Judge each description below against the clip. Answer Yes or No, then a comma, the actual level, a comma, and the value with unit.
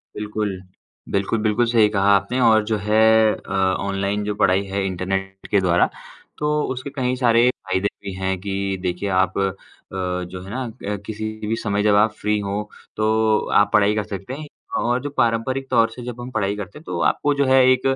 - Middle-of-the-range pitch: No, low, 105 Hz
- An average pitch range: Yes, average, 3.0 semitones